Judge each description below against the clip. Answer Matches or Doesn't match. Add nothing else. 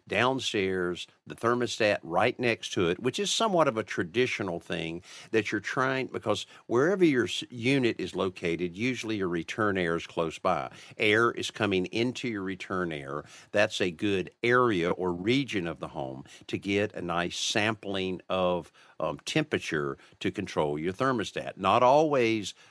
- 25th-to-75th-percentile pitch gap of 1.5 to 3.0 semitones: Doesn't match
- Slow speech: Doesn't match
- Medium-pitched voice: Doesn't match